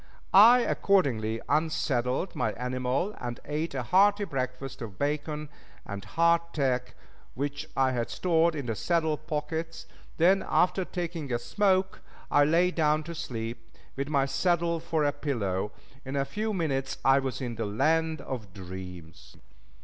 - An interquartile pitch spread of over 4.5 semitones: Yes, average, 5.1 semitones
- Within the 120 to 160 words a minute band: Yes, average, 150 wpm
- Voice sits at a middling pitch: Yes, medium, 145 Hz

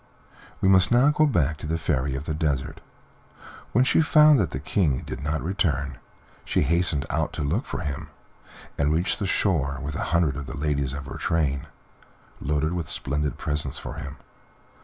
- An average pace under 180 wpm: No, average, 185 wpm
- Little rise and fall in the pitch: No, average, 3.9 semitones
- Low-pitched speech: Yes, very low, 75 Hz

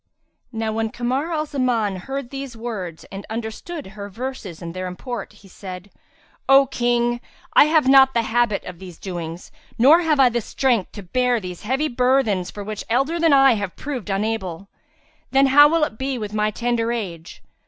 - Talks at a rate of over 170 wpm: Yes, average, 185 wpm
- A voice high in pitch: Yes, high, 235 Hz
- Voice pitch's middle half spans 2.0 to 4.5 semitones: No, average, 5.1 semitones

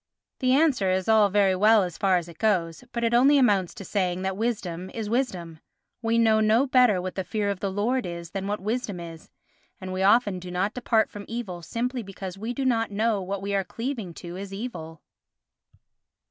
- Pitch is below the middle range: No, high, 200 Hz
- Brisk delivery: Yes, fast, 215 wpm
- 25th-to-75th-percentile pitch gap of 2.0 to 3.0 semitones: No, average, 3.8 semitones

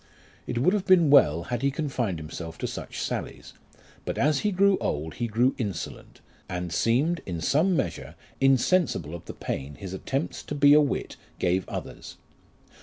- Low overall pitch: Yes, low, 125 Hz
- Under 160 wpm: No, average, 175 wpm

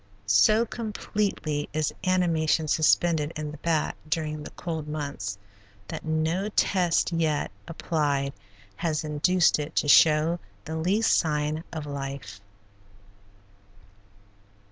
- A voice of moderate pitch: Yes, medium, 155 Hz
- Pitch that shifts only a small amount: Yes, narrow, 2.3 semitones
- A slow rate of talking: Yes, slow, 110 wpm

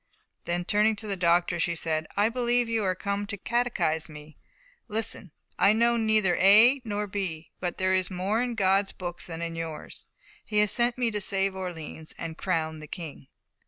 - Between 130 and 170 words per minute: No, average, 190 wpm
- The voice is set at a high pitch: Yes, high, 195 Hz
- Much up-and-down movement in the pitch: No, average, 4.3 semitones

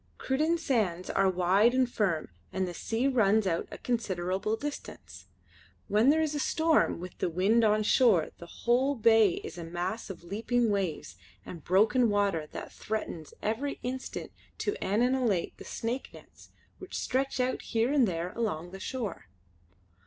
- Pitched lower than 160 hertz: No, high, 215 Hz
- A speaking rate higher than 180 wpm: No, average, 160 wpm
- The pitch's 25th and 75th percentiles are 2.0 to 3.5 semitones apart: No, wide, 5.5 semitones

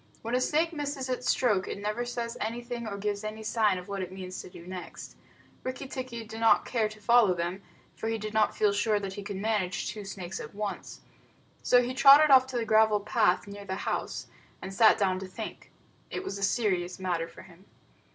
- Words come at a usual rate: No, fast, 220 wpm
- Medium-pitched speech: No, high, 215 Hz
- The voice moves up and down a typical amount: Yes, average, 3.7 semitones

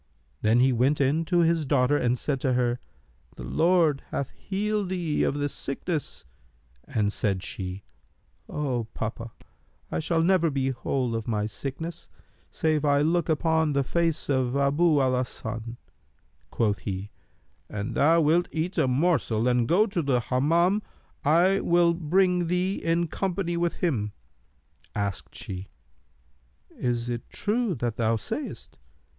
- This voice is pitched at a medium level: Yes, medium, 145 Hz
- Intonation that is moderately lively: No, wide, 5.8 semitones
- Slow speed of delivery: No, average, 150 wpm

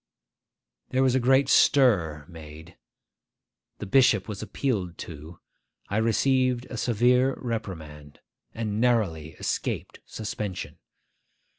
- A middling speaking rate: No, slow, 105 wpm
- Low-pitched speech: Yes, low, 110 Hz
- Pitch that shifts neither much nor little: No, wide, 7.2 semitones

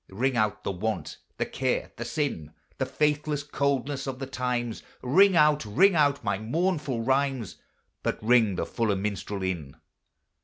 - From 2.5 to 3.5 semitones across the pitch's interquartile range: No, average, 5.1 semitones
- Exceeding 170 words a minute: No, average, 155 wpm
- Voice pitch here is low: Yes, low, 130 Hz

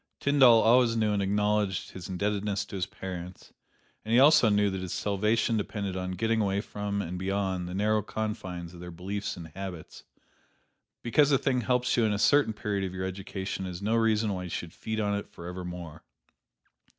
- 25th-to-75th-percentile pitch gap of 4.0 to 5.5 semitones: No, average, 2.9 semitones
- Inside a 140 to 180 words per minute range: No, average, 190 wpm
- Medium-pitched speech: No, low, 100 Hz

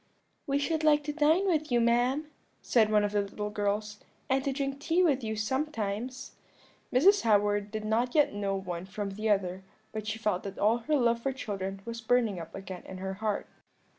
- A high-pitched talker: Yes, high, 220 Hz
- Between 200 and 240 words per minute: Yes, fast, 205 wpm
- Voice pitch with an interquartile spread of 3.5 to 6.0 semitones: Yes, average, 4.9 semitones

